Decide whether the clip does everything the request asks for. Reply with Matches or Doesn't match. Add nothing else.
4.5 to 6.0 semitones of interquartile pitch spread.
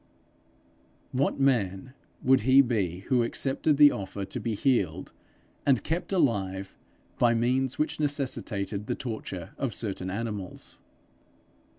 Matches